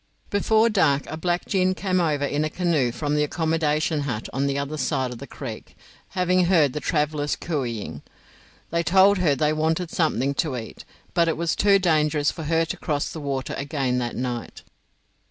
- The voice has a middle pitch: Yes, medium, 155 Hz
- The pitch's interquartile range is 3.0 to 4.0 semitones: Yes, average, 3.4 semitones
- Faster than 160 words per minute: Yes, average, 190 wpm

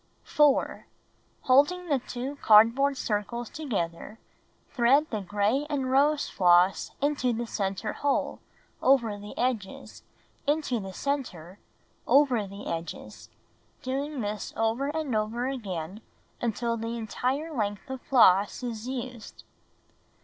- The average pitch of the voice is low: No, high, 240 Hz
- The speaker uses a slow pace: Yes, slow, 120 wpm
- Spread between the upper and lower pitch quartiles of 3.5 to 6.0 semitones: Yes, average, 4.8 semitones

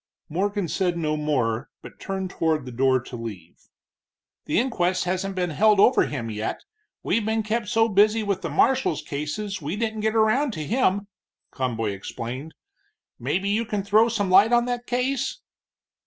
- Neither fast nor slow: Yes, average, 170 wpm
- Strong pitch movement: Yes, wide, 6.6 semitones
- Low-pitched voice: No, high, 195 Hz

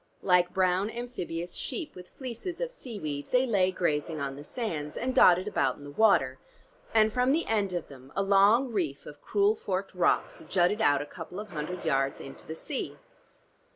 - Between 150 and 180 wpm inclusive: No, average, 190 wpm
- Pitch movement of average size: No, wide, 6.6 semitones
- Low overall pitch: No, medium, 185 Hz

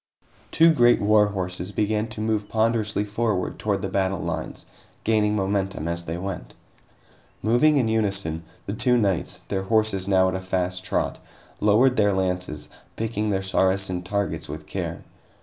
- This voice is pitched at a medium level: No, low, 100 Hz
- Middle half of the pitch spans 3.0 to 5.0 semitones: No, narrow, 2.6 semitones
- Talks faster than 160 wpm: No, average, 155 wpm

